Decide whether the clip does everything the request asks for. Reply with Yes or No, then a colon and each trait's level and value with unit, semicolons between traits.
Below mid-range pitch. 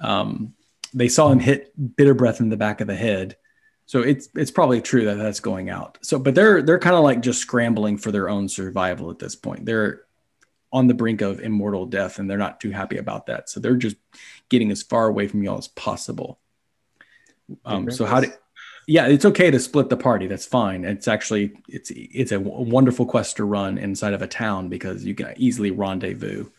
Yes: low, 110 Hz